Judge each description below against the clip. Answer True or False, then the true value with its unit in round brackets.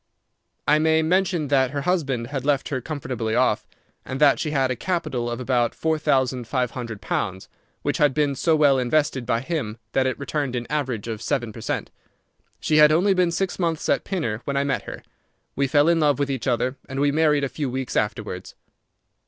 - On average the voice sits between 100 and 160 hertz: True (140 Hz)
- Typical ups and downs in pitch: True (3.6 semitones)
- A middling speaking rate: False (210 wpm)